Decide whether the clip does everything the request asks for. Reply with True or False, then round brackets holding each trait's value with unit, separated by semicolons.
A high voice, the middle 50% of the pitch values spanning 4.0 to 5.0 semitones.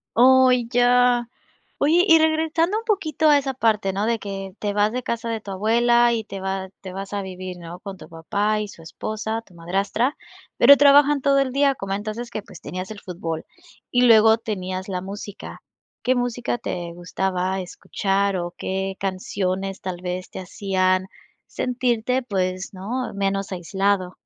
True (205 Hz; 4.5 semitones)